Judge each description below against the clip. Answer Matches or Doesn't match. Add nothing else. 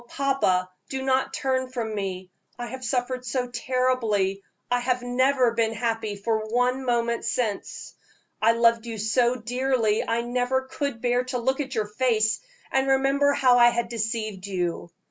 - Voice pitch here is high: Matches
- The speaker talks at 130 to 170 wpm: Matches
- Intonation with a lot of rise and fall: Doesn't match